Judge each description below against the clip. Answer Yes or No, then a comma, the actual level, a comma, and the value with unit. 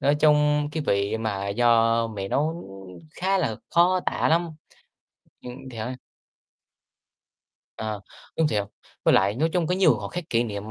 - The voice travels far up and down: Yes, wide, 6.8 semitones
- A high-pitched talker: No, low, 125 Hz